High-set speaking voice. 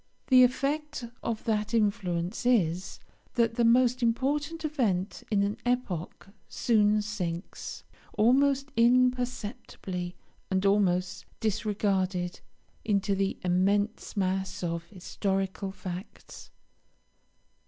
Yes: high, 210 Hz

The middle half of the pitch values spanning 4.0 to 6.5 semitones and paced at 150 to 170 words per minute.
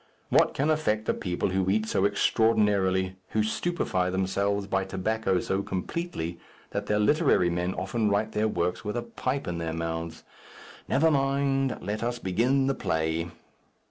Yes: average, 4.3 semitones; average, 160 wpm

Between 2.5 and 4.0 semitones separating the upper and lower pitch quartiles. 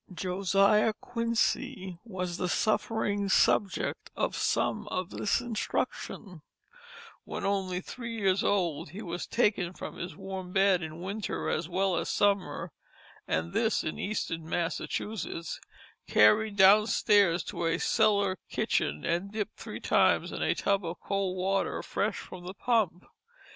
Yes: average, 2.9 semitones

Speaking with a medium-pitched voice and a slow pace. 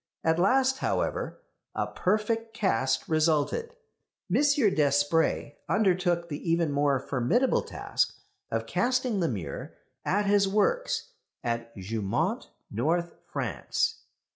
Yes: medium, 170 Hz; slow, 110 wpm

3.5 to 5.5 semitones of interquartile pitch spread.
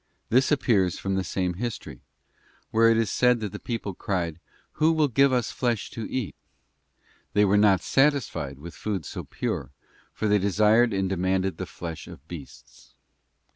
Yes: average, 4.5 semitones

